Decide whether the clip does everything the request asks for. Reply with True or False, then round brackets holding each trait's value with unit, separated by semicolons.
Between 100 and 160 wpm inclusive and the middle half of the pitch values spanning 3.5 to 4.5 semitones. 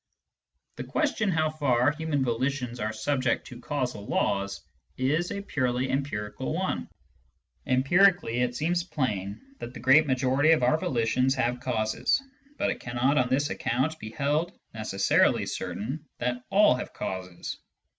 True (145 wpm; 4.0 semitones)